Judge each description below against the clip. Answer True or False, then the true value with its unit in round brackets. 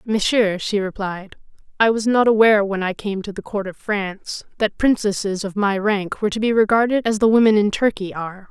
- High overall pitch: True (205 Hz)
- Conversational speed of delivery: False (210 wpm)